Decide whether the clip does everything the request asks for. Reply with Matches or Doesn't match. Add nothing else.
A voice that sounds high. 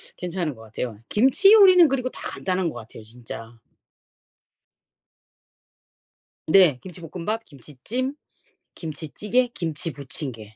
Doesn't match